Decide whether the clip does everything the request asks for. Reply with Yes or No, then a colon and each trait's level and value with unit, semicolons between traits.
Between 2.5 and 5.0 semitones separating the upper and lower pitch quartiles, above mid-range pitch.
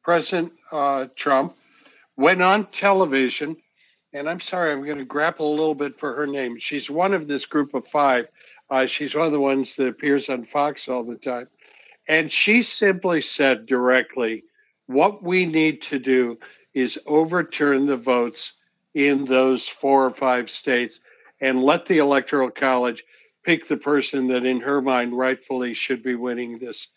No: average, 3.4 semitones; medium, 140 Hz